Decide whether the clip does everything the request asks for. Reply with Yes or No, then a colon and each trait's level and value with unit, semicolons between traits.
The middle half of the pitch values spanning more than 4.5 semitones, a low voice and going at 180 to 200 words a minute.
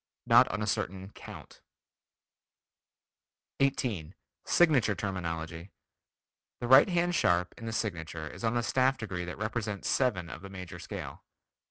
No: wide, 5.6 semitones; low, 100 Hz; average, 140 wpm